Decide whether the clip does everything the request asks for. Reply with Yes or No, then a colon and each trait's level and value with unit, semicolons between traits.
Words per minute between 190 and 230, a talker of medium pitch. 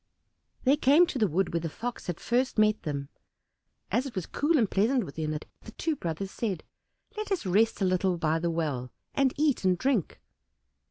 No: average, 200 wpm; high, 195 Hz